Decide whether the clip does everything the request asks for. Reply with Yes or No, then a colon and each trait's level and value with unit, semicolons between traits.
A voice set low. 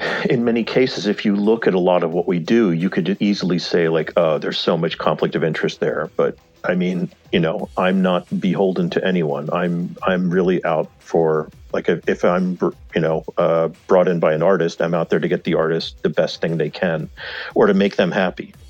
Yes: very low, 90 Hz